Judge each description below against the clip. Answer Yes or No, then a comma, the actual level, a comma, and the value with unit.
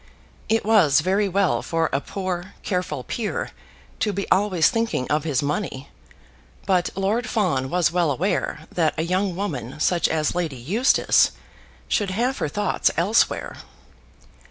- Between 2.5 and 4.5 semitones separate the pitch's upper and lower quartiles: No, average, 5.0 semitones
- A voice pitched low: No, medium, 180 Hz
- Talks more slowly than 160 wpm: Yes, average, 145 wpm